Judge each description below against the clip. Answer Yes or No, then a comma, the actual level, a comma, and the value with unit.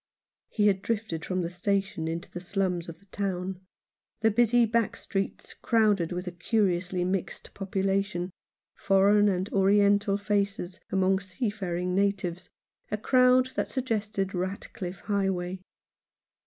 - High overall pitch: Yes, high, 195 Hz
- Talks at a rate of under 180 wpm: Yes, slow, 135 wpm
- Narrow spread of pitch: Yes, narrow, 2.2 semitones